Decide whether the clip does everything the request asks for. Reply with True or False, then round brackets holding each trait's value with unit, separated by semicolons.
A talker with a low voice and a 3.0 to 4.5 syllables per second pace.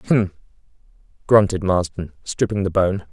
True (95 Hz; 4.4 syllables/s)